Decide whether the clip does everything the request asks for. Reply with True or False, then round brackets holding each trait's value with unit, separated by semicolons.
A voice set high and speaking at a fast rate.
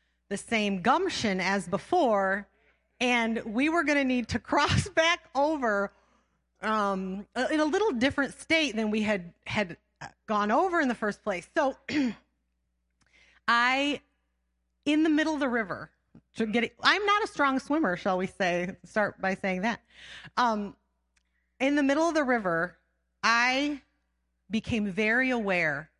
False (225 Hz; 150 wpm)